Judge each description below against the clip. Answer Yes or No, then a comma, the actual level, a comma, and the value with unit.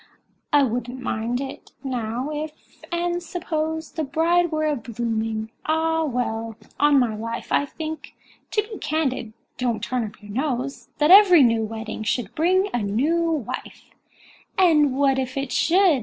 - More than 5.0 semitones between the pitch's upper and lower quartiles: Yes, wide, 5.5 semitones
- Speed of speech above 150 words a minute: No, average, 140 wpm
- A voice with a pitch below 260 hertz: No, very high, 275 Hz